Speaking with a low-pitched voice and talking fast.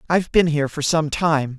No: medium, 155 Hz; fast, 225 wpm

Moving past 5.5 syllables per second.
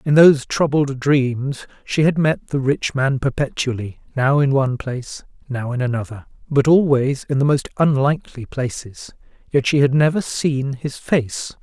No: 4.6 syllables/s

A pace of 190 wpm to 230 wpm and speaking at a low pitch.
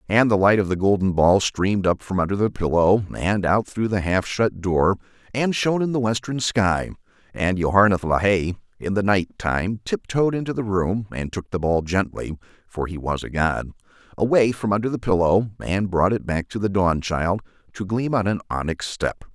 Yes: fast, 205 wpm; low, 100 Hz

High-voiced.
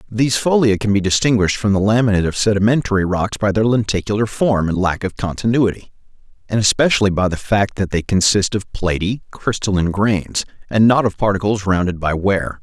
No: low, 105 Hz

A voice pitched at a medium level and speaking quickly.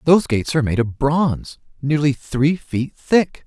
No: medium, 145 Hz; average, 175 wpm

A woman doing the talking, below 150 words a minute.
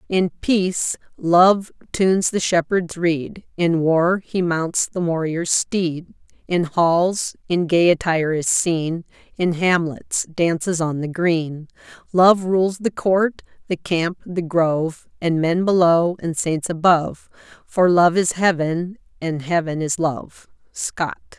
Yes: female; average, 140 wpm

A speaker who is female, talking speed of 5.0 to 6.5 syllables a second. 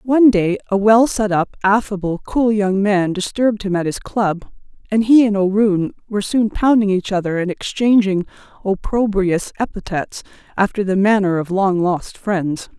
No: female; 4.7 syllables/s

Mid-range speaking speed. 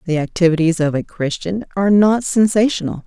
Yes: average, 155 wpm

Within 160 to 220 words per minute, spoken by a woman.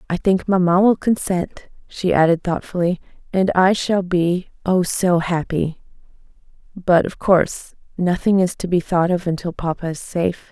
No: average, 150 wpm; female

